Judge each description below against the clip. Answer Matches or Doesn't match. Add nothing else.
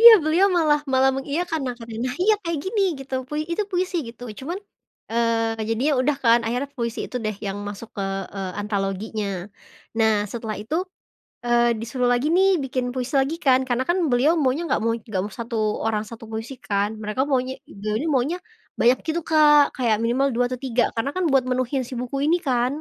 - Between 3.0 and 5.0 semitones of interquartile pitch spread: Matches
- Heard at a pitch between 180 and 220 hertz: Doesn't match